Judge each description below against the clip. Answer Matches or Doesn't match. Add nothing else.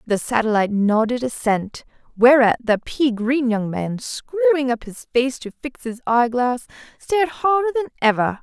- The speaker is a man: Doesn't match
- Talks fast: Doesn't match